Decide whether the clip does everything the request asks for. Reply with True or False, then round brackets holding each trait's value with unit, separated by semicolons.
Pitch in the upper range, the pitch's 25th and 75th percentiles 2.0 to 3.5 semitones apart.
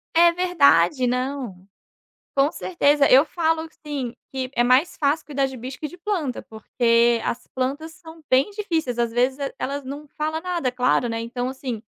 False (275 Hz; 4.3 semitones)